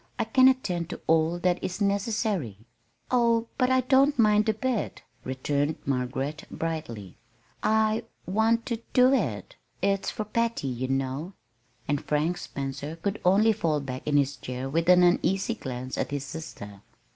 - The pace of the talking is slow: No, average, 155 wpm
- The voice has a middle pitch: Yes, medium, 175 Hz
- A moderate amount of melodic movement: No, wide, 7.8 semitones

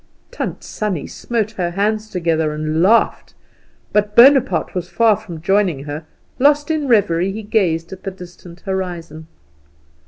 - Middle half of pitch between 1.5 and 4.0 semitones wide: No, average, 4.5 semitones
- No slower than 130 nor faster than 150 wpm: Yes, average, 145 wpm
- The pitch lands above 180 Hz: Yes, high, 190 Hz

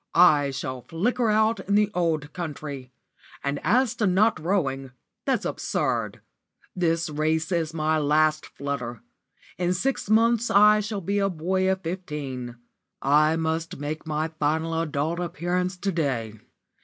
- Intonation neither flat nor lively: Yes, average, 4.2 semitones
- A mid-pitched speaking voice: Yes, medium, 165 Hz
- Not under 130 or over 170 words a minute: Yes, average, 145 wpm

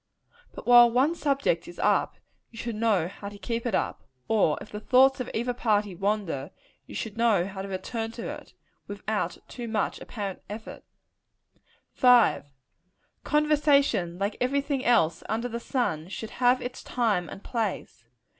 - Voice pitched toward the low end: No, high, 225 Hz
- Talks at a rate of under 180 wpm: Yes, average, 165 wpm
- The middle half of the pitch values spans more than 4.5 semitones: No, average, 3.8 semitones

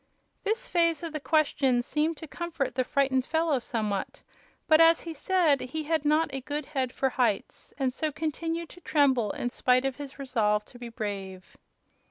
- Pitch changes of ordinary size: Yes, average, 4.2 semitones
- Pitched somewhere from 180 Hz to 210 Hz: No, very high, 280 Hz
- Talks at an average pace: Yes, average, 185 wpm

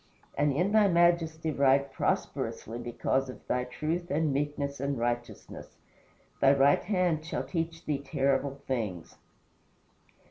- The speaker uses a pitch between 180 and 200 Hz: No, medium, 140 Hz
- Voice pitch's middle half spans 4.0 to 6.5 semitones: No, average, 3.3 semitones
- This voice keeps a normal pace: No, slow, 130 wpm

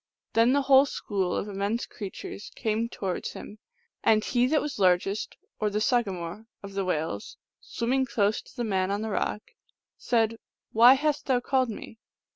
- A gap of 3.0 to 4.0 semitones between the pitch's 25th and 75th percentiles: Yes, average, 3.7 semitones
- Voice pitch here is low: No, high, 220 Hz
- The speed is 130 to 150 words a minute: No, average, 180 wpm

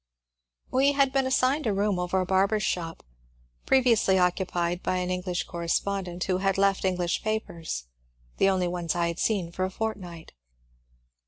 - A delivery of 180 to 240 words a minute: No, average, 165 wpm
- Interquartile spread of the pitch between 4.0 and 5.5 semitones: No, average, 3.1 semitones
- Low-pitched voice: No, medium, 185 Hz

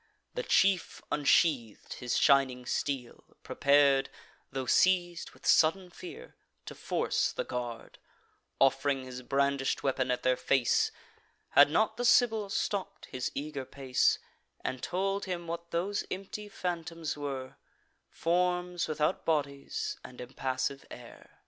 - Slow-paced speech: Yes, slow, 125 wpm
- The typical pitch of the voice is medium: Yes, medium, 145 Hz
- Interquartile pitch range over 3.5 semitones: Yes, average, 5.2 semitones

